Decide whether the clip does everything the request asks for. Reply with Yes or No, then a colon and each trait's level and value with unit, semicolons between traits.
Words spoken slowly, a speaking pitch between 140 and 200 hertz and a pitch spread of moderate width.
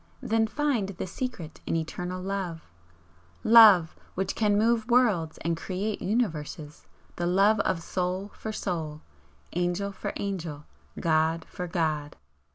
Yes: slow, 130 wpm; medium, 185 Hz; average, 4.2 semitones